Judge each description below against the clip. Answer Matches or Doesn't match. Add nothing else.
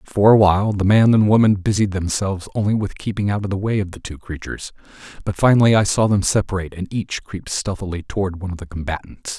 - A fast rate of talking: Matches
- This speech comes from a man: Matches